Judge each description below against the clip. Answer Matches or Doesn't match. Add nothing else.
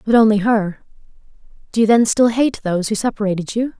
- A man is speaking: Doesn't match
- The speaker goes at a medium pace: Matches